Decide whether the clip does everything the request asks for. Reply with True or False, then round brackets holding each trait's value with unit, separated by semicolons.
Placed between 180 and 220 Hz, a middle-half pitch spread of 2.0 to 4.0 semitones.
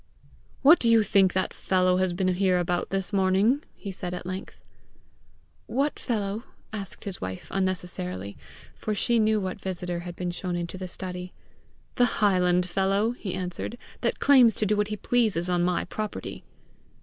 True (190 Hz; 2.9 semitones)